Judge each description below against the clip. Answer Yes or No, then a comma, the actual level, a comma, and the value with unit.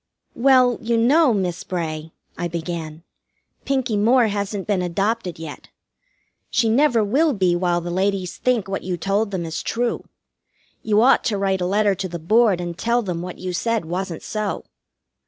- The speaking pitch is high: Yes, high, 195 Hz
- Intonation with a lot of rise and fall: No, average, 4.6 semitones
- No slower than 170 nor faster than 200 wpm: Yes, average, 175 wpm